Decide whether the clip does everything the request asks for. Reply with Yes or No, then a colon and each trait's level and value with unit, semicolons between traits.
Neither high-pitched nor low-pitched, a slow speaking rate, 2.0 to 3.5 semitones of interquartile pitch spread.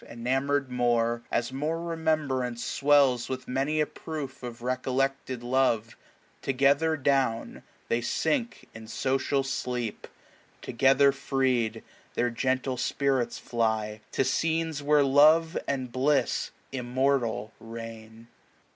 No: low, 130 Hz; slow, 120 wpm; average, 2.9 semitones